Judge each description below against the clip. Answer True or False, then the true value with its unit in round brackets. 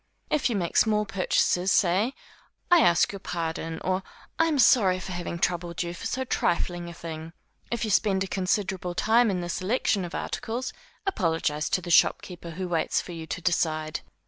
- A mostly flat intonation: False (3.5 semitones)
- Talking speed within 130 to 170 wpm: False (185 wpm)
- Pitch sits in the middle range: True (180 Hz)